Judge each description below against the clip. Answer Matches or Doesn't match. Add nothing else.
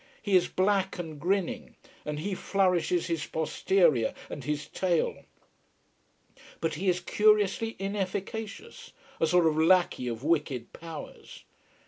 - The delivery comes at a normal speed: Doesn't match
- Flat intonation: Doesn't match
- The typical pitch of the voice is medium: Matches